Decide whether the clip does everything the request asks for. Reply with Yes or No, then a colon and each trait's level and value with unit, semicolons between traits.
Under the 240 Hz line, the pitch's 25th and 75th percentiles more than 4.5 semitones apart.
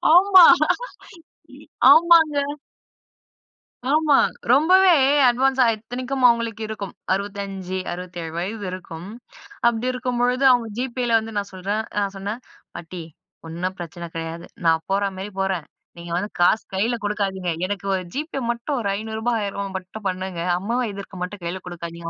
Yes: high, 205 Hz; average, 5.1 semitones